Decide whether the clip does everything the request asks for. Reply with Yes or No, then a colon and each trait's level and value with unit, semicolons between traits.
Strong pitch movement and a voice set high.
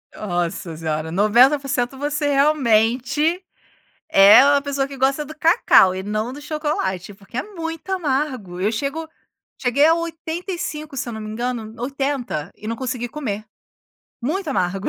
Yes: wide, 5.8 semitones; very high, 260 Hz